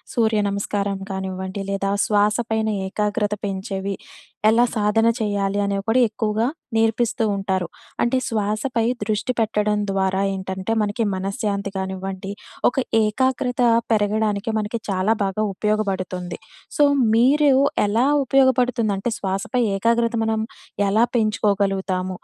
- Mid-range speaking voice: No, high, 210 Hz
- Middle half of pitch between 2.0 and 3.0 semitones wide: Yes, narrow, 2.4 semitones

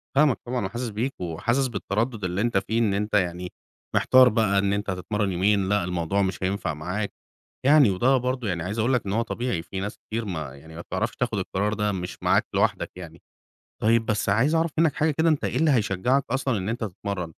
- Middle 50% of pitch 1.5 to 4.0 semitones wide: No, average, 4.5 semitones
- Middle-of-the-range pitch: No, low, 105 Hz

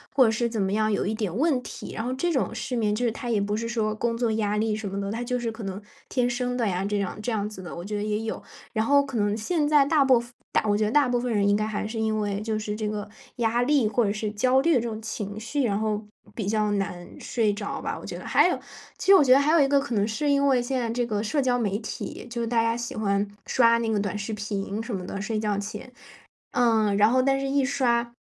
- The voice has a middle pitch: No, high, 225 Hz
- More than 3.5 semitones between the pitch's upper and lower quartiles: No, average, 2.9 semitones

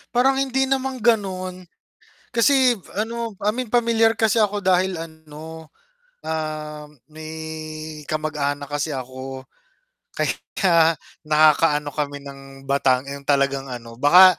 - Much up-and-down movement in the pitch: Yes, wide, 6.9 semitones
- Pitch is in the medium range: Yes, medium, 160 Hz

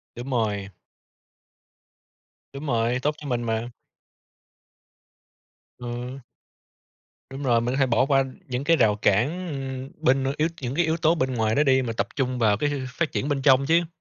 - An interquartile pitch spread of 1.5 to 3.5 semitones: Yes, average, 3.1 semitones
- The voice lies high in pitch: No, low, 130 Hz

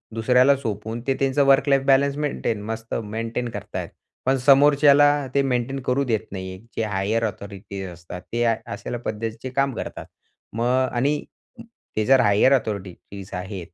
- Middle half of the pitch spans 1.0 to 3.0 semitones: No, average, 4.4 semitones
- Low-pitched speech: Yes, low, 120 Hz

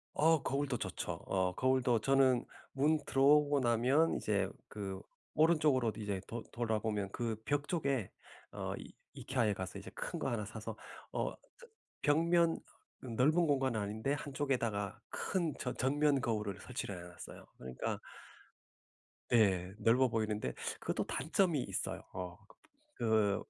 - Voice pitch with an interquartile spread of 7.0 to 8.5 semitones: No, wide, 5.4 semitones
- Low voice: Yes, low, 120 Hz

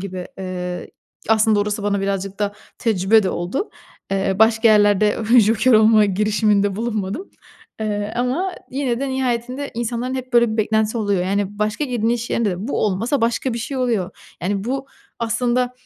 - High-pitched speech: Yes, high, 220 Hz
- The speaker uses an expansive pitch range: No, average, 3.0 semitones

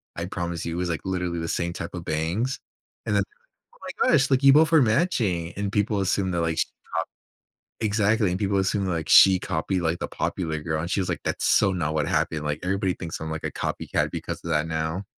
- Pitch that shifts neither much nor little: Yes, average, 3.6 semitones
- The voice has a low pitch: Yes, very low, 90 Hz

